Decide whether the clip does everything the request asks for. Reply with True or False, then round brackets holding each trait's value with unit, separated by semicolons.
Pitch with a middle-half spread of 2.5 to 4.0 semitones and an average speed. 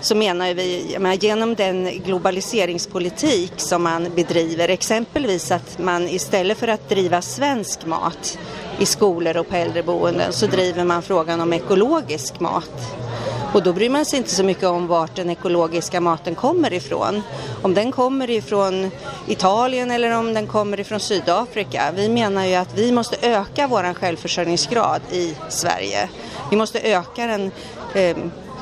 True (3.6 semitones; 150 wpm)